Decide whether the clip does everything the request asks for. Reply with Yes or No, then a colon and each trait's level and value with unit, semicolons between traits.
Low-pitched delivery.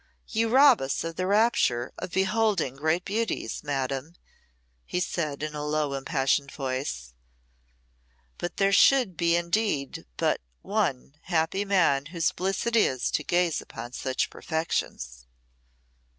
No: medium, 165 Hz